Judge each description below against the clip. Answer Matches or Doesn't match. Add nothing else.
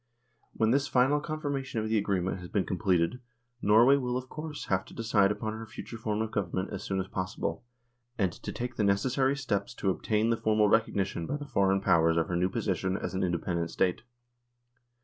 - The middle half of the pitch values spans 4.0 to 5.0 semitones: Matches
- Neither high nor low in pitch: Doesn't match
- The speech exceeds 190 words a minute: Matches